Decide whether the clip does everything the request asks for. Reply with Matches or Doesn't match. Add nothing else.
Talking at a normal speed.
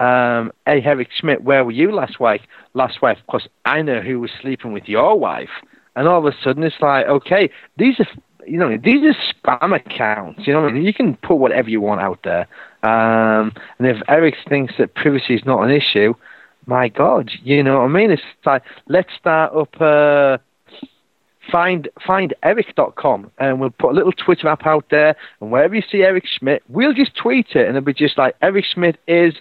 Doesn't match